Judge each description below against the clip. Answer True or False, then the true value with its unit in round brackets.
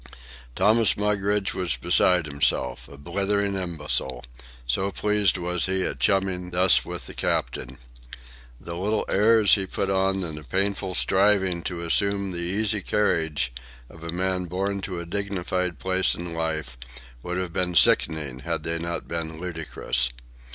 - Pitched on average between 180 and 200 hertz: False (90 Hz)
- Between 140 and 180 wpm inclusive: True (150 wpm)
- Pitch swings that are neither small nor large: True (3.1 semitones)